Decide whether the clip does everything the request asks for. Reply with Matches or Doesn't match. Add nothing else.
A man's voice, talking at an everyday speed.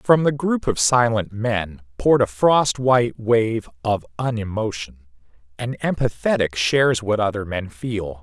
Matches